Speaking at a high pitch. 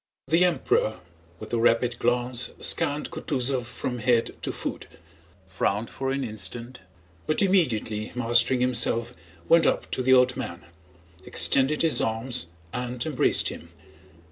No: low, 125 Hz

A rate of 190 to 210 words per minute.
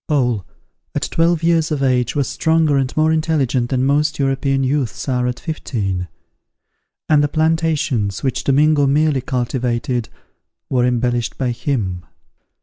No: average, 140 wpm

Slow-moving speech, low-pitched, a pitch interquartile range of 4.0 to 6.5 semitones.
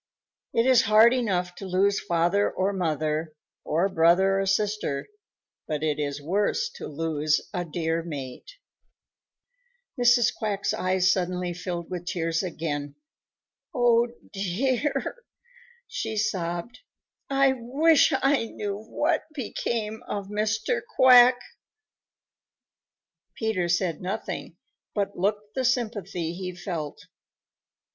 No: slow, 110 wpm; high, 195 Hz; average, 5.0 semitones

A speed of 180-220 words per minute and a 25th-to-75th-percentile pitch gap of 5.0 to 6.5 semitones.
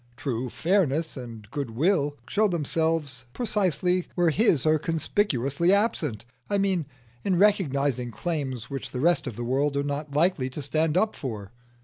No: average, 150 wpm; average, 5.3 semitones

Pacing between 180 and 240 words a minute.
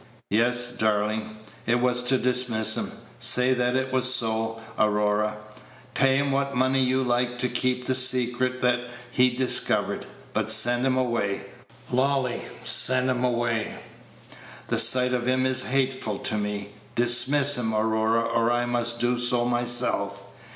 No: average, 150 wpm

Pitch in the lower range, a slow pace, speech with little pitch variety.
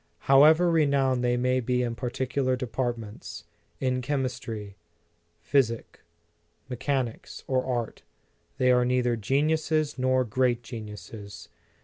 Yes: low, 125 Hz; slow, 115 wpm; narrow, 2.1 semitones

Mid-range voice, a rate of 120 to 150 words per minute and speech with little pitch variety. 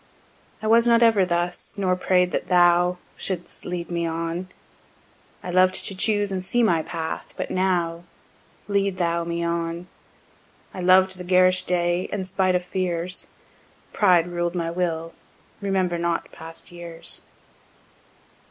Yes: medium, 180 Hz; average, 145 wpm; narrow, 1.6 semitones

